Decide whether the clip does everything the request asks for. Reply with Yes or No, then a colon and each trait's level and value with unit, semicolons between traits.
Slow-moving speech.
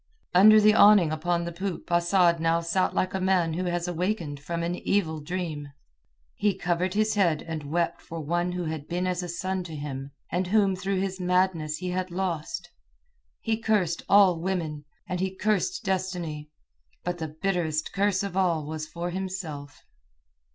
No: average, 175 wpm